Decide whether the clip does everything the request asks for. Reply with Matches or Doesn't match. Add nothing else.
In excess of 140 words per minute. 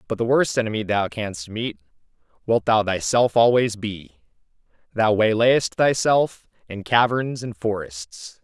Doesn't match